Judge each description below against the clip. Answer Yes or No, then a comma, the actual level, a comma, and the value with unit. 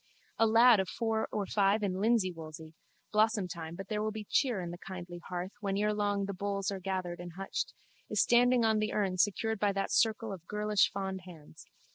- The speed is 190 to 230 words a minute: Yes, average, 200 wpm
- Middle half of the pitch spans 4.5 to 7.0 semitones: No, average, 2.8 semitones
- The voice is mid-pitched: No, high, 200 Hz